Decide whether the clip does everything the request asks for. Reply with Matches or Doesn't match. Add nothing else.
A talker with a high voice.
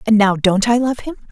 Matches